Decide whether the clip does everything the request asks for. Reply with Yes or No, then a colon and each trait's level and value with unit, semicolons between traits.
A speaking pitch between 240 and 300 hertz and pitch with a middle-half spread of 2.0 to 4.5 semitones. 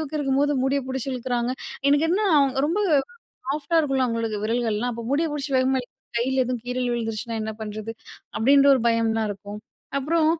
Yes: very high, 255 Hz; average, 3.7 semitones